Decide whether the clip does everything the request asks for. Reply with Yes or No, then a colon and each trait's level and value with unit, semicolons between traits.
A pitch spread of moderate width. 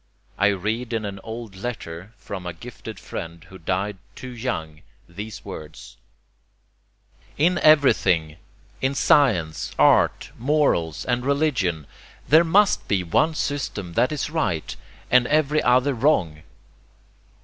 No: wide, 7.7 semitones